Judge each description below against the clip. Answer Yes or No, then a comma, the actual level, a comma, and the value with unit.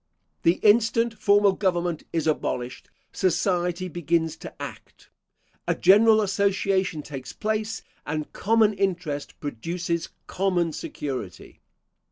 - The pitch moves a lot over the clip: No, average, 3.9 semitones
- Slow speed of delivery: Yes, slow, 105 wpm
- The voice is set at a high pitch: No, medium, 180 Hz